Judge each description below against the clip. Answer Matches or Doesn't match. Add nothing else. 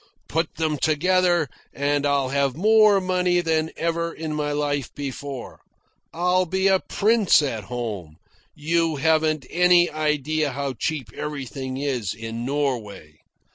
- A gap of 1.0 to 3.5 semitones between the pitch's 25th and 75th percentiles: Doesn't match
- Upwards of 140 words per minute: Doesn't match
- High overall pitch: Doesn't match